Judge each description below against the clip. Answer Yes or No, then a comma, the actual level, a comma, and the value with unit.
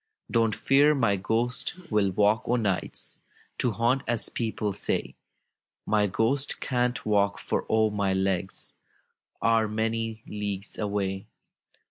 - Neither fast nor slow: No, slow, 125 wpm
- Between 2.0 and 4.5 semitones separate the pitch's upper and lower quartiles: Yes, narrow, 2.4 semitones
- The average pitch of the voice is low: Yes, low, 110 Hz